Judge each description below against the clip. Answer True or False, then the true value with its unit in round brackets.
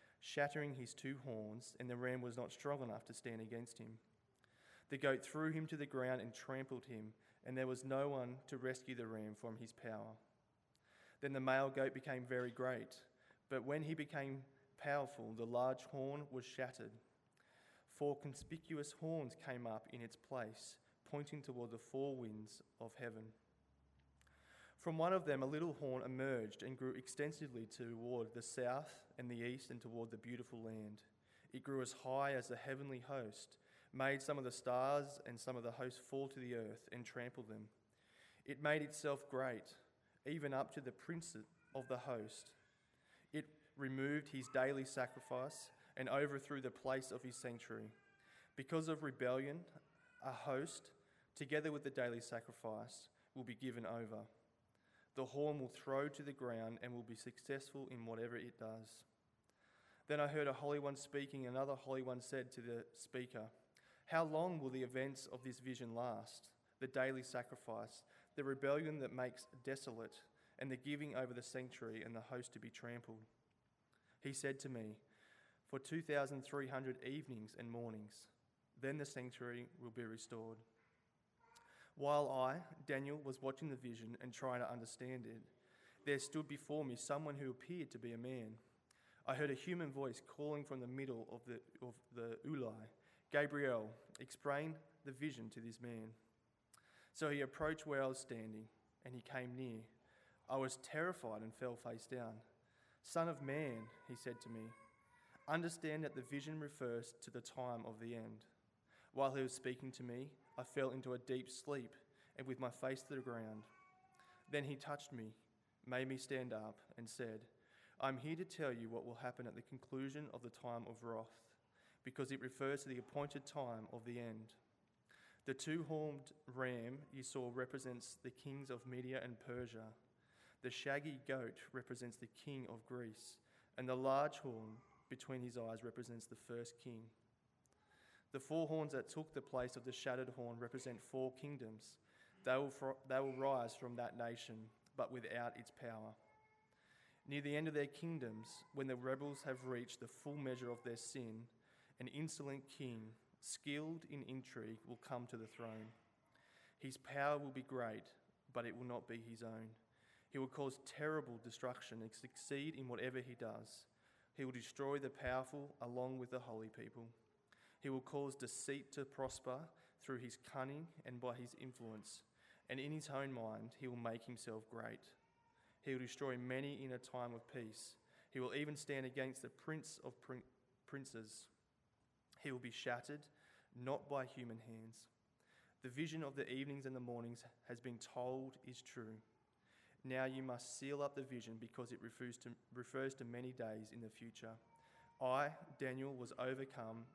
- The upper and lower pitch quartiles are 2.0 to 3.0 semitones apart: True (2.7 semitones)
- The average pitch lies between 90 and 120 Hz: False (130 Hz)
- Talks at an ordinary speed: True (170 wpm)